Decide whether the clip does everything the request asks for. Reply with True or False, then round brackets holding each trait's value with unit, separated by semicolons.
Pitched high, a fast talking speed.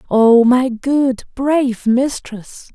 False (250 Hz; 110 wpm)